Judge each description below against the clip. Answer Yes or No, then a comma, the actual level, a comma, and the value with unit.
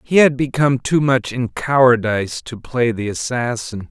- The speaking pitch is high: No, low, 125 Hz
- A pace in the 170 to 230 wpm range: No, average, 155 wpm